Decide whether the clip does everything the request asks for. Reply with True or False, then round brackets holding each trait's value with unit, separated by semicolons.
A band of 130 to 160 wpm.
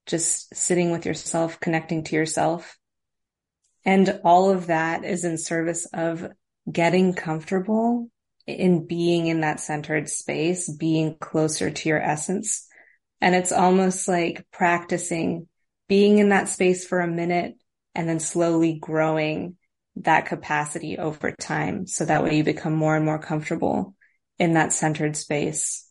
True (140 wpm)